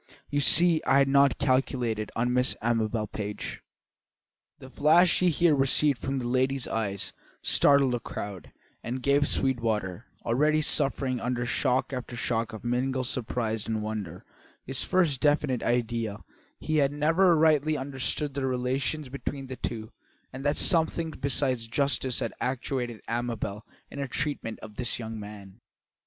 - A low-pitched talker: Yes, low, 130 Hz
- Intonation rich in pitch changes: No, average, 3.6 semitones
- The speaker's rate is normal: Yes, average, 150 wpm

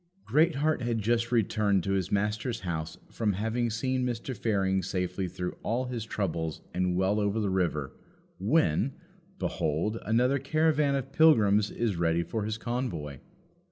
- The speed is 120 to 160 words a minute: Yes, average, 150 wpm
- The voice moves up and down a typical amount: Yes, average, 4.6 semitones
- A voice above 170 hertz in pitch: No, low, 105 Hz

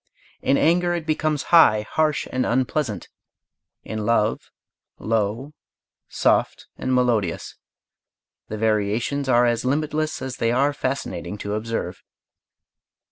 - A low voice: Yes, low, 125 Hz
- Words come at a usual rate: No, slow, 115 wpm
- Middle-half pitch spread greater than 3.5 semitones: Yes, average, 5.1 semitones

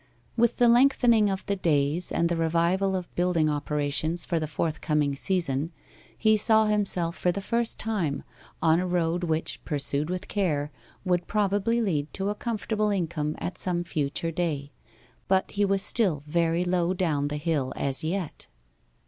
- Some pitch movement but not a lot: Yes, average, 4.3 semitones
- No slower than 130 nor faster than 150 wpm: No, average, 165 wpm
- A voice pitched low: No, medium, 175 Hz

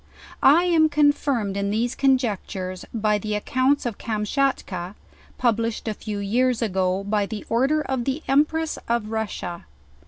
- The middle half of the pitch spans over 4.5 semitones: Yes, average, 4.9 semitones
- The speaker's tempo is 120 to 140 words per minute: Yes, slow, 135 wpm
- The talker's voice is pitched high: Yes, high, 230 Hz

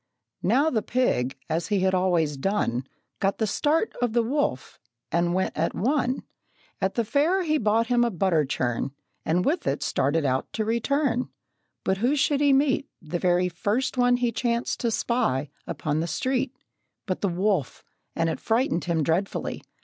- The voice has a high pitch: Yes, high, 210 Hz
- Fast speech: No, average, 175 wpm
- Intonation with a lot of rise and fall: Yes, wide, 7.0 semitones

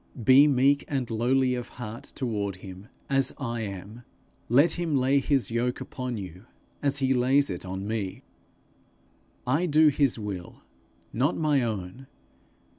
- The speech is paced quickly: No, average, 145 wpm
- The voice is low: Yes, low, 125 Hz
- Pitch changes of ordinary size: Yes, average, 4.5 semitones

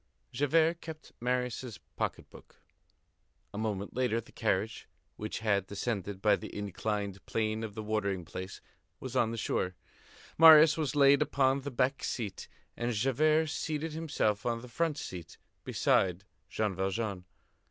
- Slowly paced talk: No, average, 145 wpm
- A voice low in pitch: Yes, low, 115 Hz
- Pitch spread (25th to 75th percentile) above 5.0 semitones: Yes, wide, 5.4 semitones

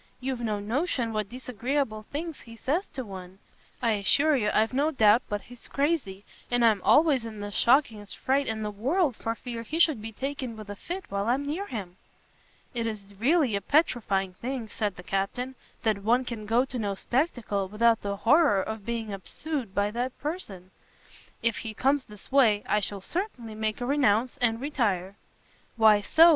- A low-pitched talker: No, high, 230 Hz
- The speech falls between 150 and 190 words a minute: Yes, average, 185 wpm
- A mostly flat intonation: No, average, 4.6 semitones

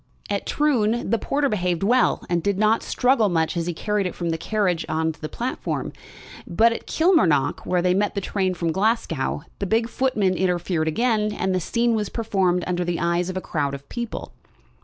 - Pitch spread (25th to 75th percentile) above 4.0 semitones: Yes, average, 4.7 semitones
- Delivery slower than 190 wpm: No, average, 200 wpm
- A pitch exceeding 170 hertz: Yes, high, 190 Hz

